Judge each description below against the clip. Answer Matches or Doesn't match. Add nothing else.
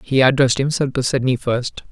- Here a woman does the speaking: Doesn't match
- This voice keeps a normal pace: Matches